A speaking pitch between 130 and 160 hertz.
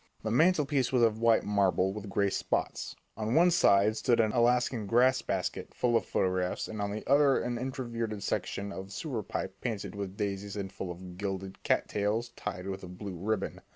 No: low, 105 Hz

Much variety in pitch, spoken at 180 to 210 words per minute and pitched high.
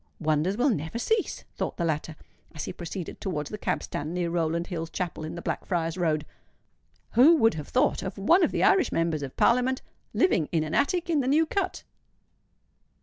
No: wide, 7.9 semitones; average, 195 wpm; medium, 175 Hz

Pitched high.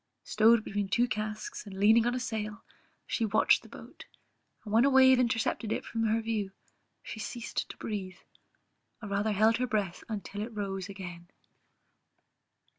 Yes: high, 215 Hz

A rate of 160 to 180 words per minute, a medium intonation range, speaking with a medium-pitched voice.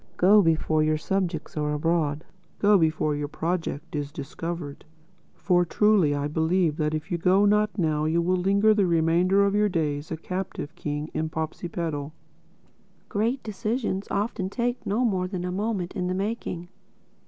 Yes: average, 165 wpm; average, 4.2 semitones; medium, 175 Hz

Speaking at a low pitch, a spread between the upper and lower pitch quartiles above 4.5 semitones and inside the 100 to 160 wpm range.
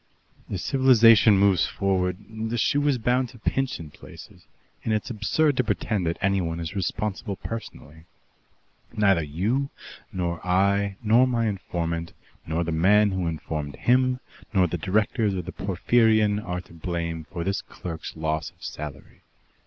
Yes: low, 100 Hz; average, 4.9 semitones; average, 155 wpm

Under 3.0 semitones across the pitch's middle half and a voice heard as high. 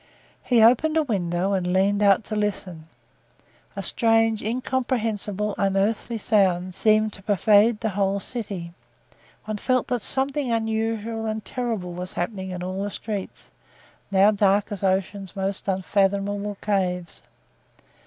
Yes: narrow, 2.6 semitones; high, 205 Hz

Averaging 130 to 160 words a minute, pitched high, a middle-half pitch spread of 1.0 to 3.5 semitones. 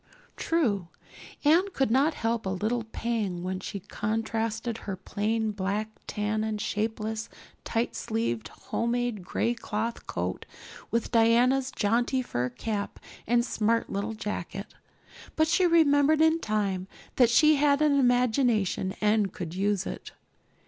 Yes: slow, 135 wpm; high, 225 Hz; average, 3.0 semitones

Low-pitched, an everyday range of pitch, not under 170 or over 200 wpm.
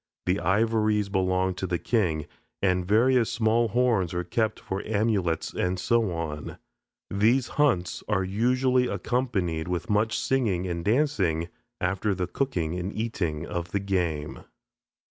No: low, 100 Hz; average, 4.5 semitones; average, 140 wpm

